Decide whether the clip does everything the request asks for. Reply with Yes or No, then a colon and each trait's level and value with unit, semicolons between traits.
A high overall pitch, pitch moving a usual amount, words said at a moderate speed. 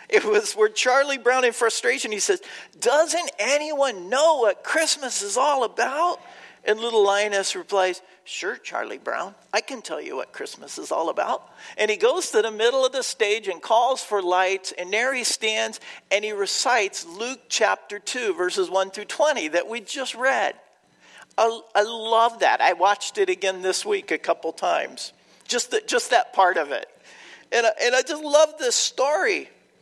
No: high, 240 Hz; wide, 8.3 semitones; average, 185 wpm